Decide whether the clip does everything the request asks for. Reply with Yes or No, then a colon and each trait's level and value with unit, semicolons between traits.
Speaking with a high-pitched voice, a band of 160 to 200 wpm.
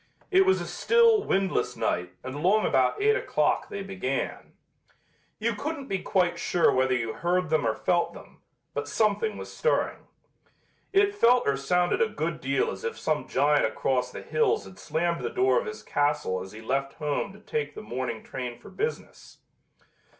No: medium, 170 Hz; average, 180 wpm